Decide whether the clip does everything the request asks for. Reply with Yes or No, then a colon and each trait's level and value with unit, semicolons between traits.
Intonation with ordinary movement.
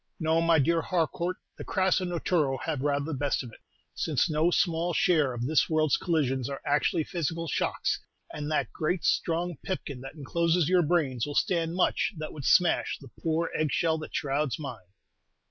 Yes: average, 3.1 semitones